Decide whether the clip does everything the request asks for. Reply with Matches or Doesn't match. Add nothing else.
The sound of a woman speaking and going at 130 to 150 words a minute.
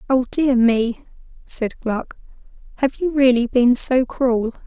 Matches